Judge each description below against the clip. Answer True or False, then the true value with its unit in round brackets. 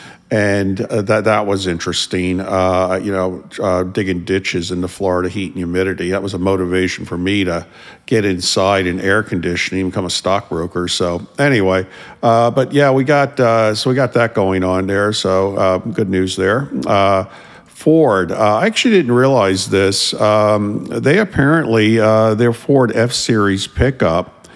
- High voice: False (100 Hz)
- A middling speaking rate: True (170 wpm)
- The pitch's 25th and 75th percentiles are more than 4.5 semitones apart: False (3.3 semitones)